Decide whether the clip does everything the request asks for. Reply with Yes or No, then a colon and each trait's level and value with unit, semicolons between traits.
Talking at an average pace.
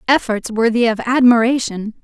No: slow, 120 wpm